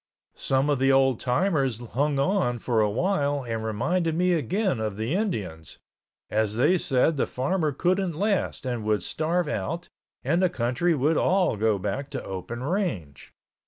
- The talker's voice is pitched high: No, low, 135 Hz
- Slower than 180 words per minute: Yes, average, 160 wpm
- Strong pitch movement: Yes, wide, 7.5 semitones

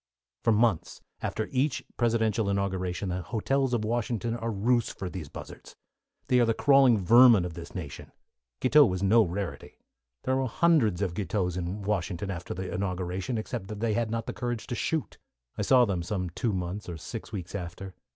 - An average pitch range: Yes, average, 4.4 semitones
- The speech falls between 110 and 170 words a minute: No, average, 185 wpm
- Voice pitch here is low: Yes, low, 105 Hz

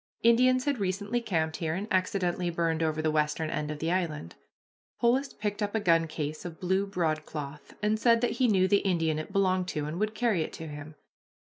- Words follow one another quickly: Yes, fast, 210 wpm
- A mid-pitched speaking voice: Yes, medium, 180 Hz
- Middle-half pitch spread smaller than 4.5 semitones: No, average, 4.8 semitones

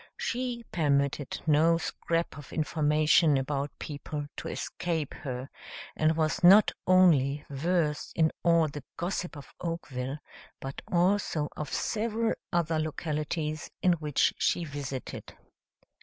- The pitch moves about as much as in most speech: Yes, average, 3.0 semitones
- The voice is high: No, medium, 155 Hz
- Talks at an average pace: No, slow, 120 wpm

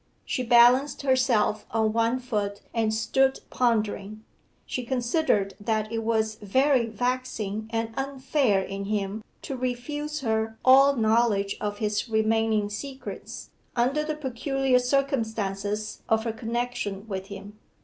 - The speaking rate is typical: No, slow, 130 wpm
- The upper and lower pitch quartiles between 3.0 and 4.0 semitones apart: Yes, average, 3.3 semitones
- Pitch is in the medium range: No, high, 225 Hz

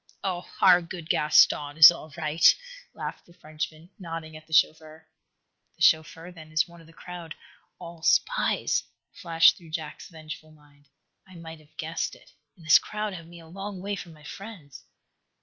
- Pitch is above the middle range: No, medium, 165 Hz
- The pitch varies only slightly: Yes, narrow, 1.8 semitones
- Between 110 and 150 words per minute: No, average, 175 wpm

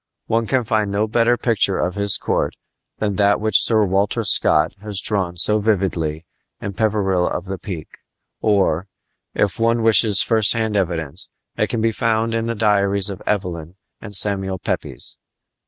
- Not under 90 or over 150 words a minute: No, average, 170 wpm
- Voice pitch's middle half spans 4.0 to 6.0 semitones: No, average, 2.8 semitones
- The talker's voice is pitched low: Yes, low, 100 Hz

